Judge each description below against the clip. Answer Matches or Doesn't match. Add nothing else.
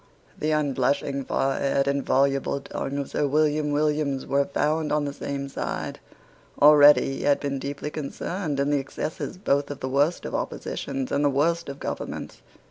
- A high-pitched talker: Doesn't match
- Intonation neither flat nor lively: Doesn't match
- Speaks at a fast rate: Doesn't match